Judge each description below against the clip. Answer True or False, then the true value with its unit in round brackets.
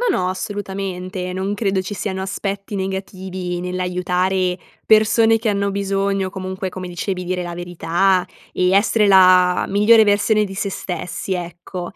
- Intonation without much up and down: True (1.6 semitones)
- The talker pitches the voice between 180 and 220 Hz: True (190 Hz)